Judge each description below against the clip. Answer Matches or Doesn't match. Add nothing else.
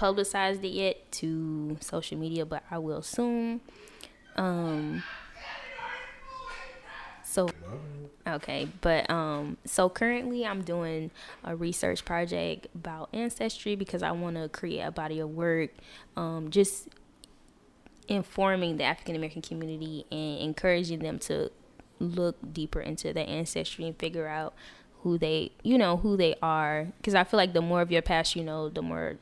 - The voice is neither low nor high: Matches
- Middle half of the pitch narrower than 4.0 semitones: Matches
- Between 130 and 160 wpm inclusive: Matches